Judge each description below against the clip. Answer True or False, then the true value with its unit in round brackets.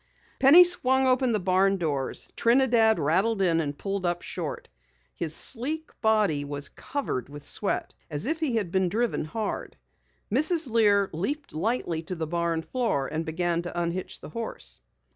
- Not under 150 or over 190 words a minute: True (160 wpm)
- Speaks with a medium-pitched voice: False (195 Hz)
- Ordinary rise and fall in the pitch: False (6.6 semitones)